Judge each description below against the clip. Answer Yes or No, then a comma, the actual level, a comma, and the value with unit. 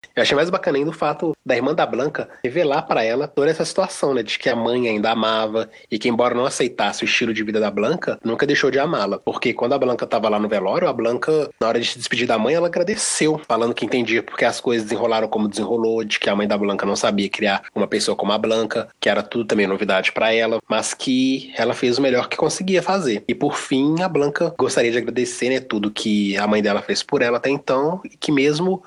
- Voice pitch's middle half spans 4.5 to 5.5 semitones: Yes, average, 4.9 semitones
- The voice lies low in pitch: Yes, low, 115 Hz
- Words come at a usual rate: No, fast, 245 wpm